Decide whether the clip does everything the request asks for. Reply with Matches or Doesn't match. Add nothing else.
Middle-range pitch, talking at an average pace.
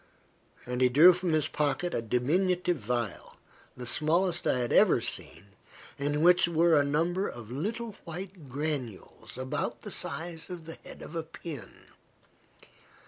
Matches